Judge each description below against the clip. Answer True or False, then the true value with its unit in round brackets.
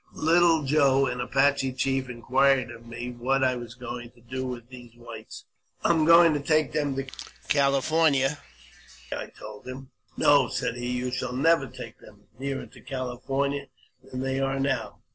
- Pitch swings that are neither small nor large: False (2.2 semitones)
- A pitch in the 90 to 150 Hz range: True (135 Hz)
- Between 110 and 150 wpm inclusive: False (180 wpm)